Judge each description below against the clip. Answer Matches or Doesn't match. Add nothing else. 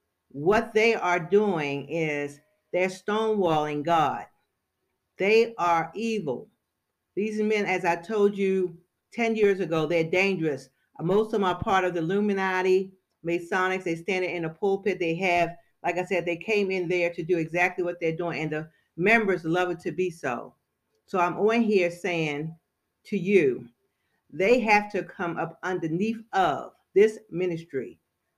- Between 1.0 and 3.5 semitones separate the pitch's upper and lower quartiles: Matches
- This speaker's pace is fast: Doesn't match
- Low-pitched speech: Doesn't match